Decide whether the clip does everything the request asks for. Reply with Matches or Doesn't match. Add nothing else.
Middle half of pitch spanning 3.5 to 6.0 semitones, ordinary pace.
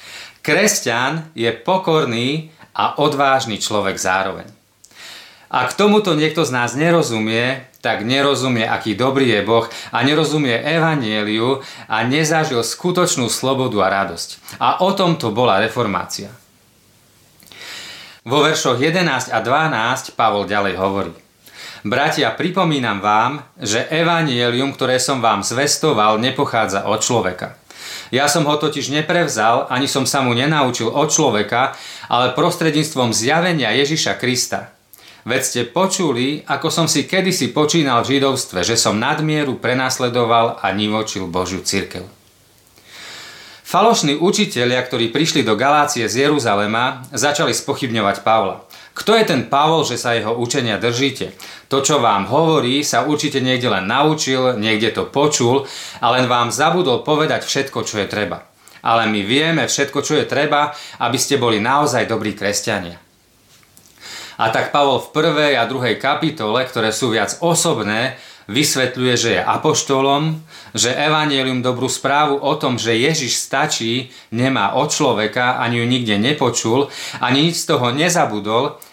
Matches